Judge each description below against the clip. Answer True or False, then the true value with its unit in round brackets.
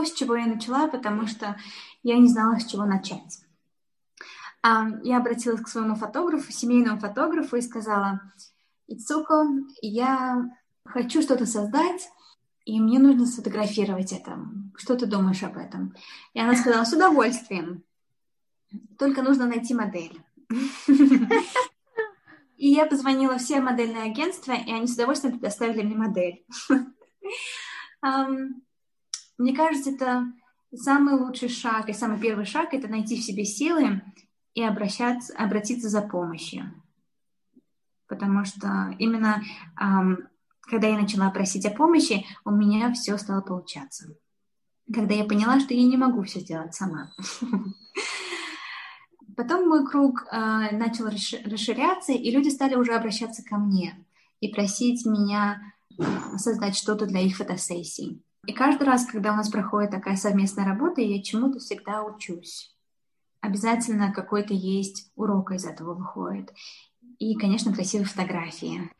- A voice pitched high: True (225 Hz)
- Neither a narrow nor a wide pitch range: True (3.9 semitones)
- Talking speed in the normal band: True (130 wpm)